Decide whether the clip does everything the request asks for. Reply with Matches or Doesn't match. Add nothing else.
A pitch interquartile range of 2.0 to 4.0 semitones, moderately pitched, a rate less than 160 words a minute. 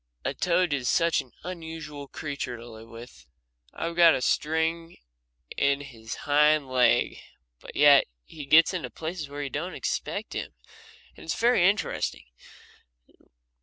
Matches